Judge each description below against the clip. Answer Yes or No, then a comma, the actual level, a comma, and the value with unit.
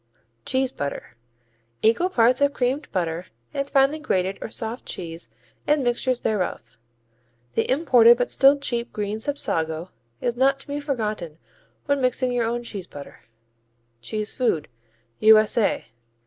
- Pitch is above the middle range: Yes, high, 235 Hz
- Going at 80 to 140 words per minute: Yes, slow, 135 wpm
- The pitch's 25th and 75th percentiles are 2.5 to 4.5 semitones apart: No, wide, 5.6 semitones